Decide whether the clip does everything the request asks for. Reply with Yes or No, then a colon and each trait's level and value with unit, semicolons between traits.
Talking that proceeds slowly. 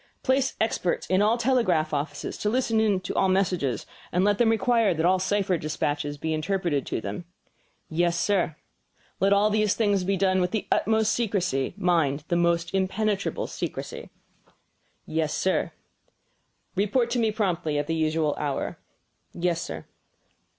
No: average, 155 wpm